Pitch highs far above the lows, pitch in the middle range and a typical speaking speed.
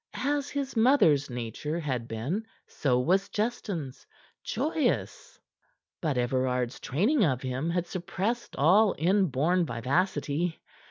No: wide, 7.4 semitones; medium, 165 Hz; slow, 110 wpm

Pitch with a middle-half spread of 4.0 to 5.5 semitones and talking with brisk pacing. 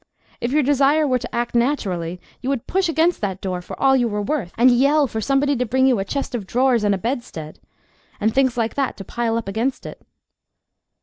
Yes: average, 4.4 semitones; fast, 225 wpm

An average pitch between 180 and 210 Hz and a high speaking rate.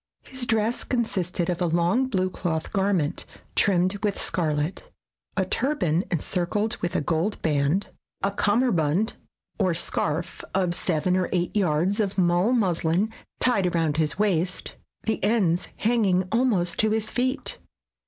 No: medium, 185 Hz; average, 140 wpm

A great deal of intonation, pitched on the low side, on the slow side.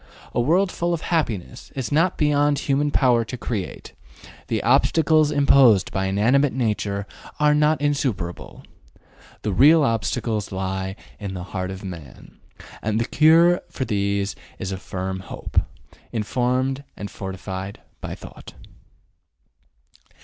Yes: wide, 7.1 semitones; low, 115 Hz; slow, 130 wpm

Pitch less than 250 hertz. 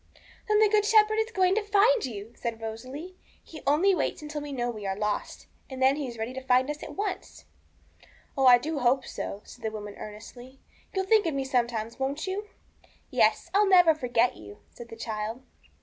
No: very high, 265 Hz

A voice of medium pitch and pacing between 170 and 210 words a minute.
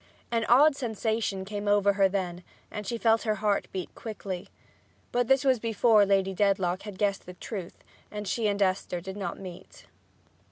No: high, 205 Hz; average, 175 wpm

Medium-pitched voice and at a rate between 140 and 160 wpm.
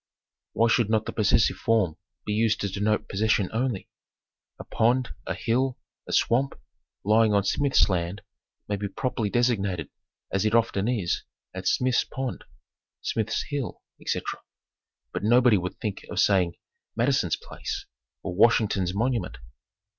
No: low, 110 Hz; average, 145 wpm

